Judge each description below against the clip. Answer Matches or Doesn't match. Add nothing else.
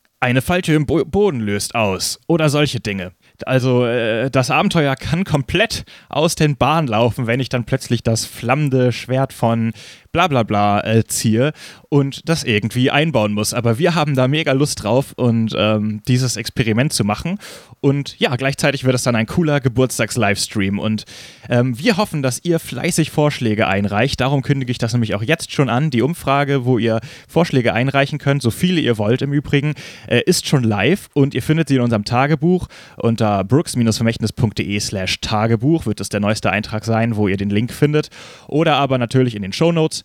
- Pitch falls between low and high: Doesn't match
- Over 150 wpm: Matches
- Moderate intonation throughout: Matches